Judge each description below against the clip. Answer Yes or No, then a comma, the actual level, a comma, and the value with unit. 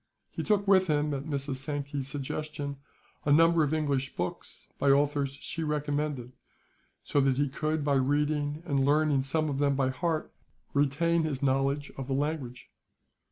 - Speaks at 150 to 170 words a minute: Yes, average, 160 wpm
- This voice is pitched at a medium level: Yes, medium, 145 Hz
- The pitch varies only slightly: Yes, narrow, 1.9 semitones